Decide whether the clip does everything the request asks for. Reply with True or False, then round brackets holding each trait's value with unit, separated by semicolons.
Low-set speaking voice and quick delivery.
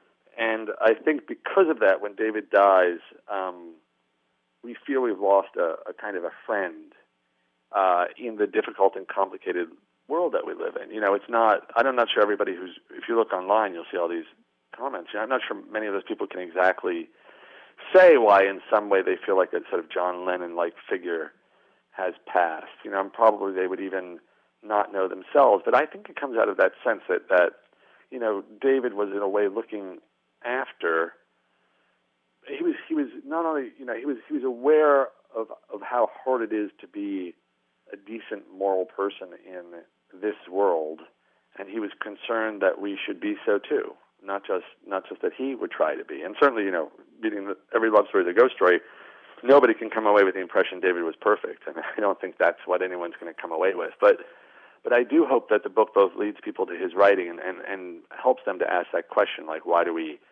False (150 Hz; 215 wpm)